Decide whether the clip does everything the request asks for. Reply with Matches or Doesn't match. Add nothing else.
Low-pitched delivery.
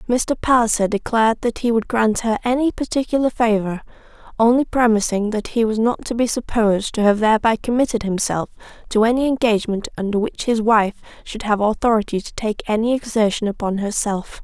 Doesn't match